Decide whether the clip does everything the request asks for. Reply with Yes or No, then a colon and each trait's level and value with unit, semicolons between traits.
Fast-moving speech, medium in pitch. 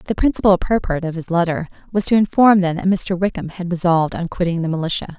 Yes: fast, 220 wpm; medium, 175 Hz